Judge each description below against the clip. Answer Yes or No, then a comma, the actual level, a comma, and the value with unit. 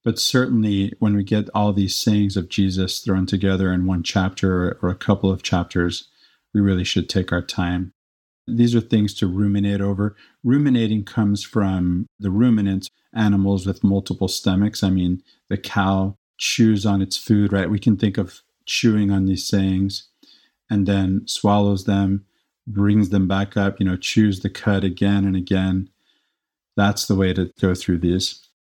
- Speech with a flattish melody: Yes, narrow, 1.8 semitones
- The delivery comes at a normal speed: Yes, average, 170 wpm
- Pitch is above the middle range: No, low, 100 Hz